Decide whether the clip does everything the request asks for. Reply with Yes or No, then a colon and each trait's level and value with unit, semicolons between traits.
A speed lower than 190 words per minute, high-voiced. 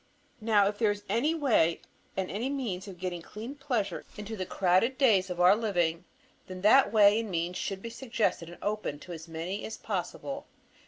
No: average, 195 wpm; high, 205 Hz